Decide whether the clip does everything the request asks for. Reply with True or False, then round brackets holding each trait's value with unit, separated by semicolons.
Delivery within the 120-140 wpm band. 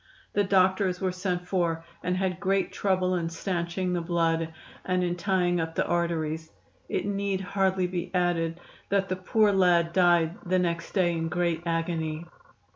False (165 wpm)